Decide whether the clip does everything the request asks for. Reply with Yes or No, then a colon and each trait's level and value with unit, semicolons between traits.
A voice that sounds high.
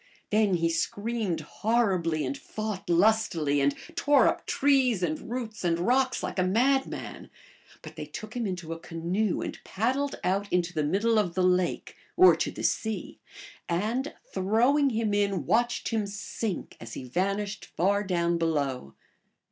Yes: high, 200 Hz